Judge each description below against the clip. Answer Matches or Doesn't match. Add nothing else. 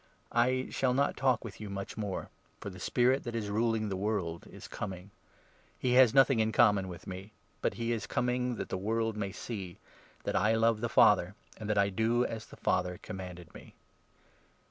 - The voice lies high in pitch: Doesn't match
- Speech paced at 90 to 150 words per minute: Doesn't match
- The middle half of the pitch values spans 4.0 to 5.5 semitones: Doesn't match